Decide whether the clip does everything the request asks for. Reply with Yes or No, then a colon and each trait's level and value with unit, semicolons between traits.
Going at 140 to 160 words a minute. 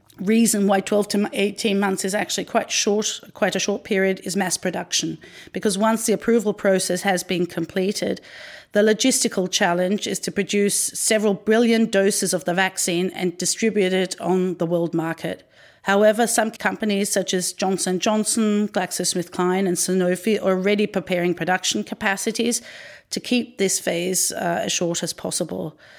Yes: average, 155 wpm